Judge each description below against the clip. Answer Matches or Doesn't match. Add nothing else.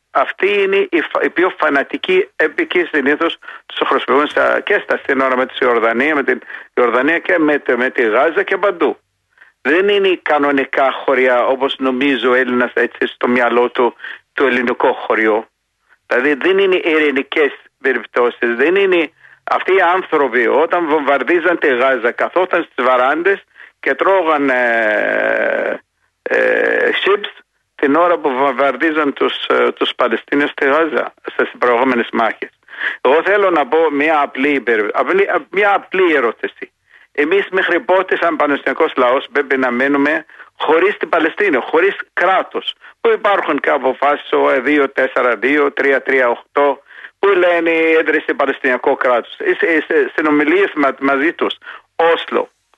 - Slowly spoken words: Doesn't match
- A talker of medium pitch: Matches